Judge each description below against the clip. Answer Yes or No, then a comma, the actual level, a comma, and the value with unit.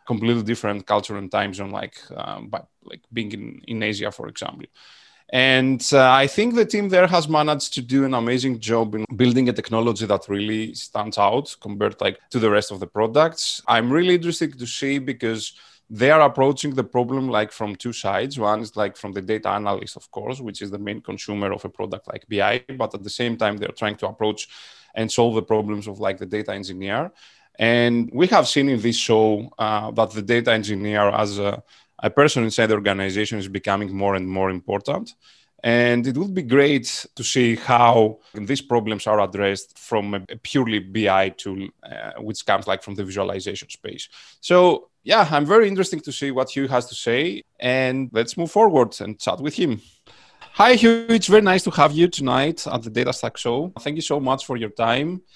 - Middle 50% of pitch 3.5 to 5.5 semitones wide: Yes, average, 4.4 semitones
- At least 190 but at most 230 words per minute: Yes, fast, 205 wpm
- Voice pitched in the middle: No, low, 115 Hz